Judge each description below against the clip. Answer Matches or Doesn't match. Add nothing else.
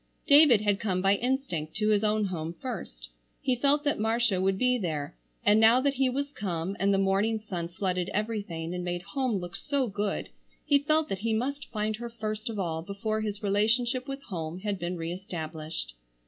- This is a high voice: Matches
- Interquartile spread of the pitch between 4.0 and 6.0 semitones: Matches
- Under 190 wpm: Doesn't match